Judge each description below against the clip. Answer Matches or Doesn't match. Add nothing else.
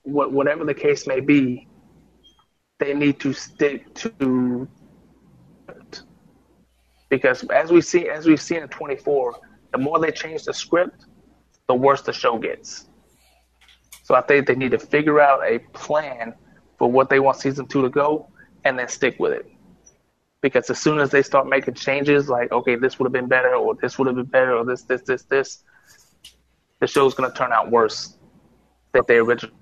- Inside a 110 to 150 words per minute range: Doesn't match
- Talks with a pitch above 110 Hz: Matches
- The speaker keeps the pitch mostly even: Doesn't match